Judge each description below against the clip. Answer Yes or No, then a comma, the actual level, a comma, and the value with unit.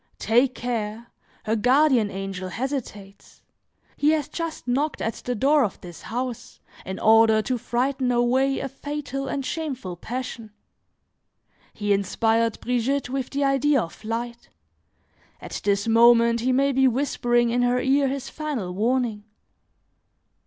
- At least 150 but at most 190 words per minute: No, average, 140 wpm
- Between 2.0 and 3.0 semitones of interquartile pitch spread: No, average, 3.4 semitones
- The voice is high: Yes, high, 245 Hz